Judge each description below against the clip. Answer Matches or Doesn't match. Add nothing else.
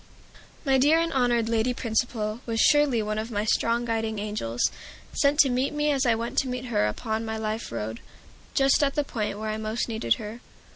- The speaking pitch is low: Doesn't match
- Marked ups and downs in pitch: Doesn't match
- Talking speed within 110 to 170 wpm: Doesn't match